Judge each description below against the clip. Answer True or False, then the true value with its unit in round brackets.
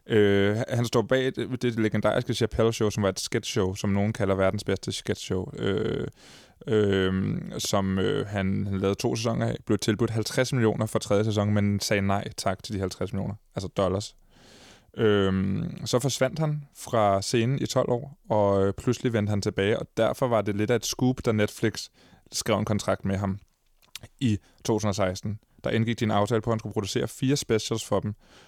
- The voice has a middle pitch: False (105 Hz)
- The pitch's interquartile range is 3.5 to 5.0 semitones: False (3.0 semitones)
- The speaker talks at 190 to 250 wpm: True (195 wpm)